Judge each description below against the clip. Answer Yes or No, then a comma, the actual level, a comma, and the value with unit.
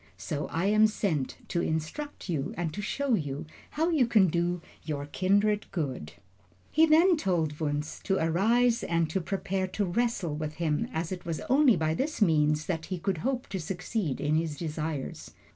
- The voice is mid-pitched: Yes, medium, 175 Hz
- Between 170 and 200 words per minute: Yes, average, 180 wpm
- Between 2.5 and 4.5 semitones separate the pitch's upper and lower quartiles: No, wide, 5.4 semitones